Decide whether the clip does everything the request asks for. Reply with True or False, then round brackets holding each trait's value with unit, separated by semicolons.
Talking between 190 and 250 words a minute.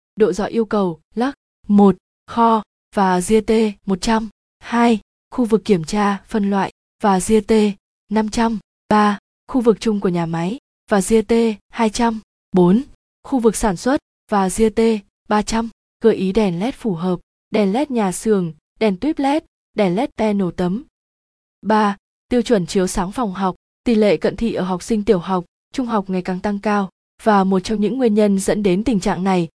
False (180 wpm)